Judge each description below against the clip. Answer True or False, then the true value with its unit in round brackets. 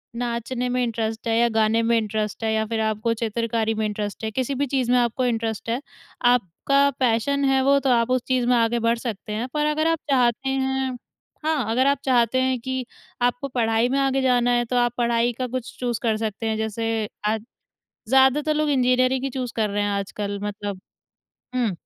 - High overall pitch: True (240 Hz)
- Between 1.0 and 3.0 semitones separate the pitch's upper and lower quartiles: True (2.7 semitones)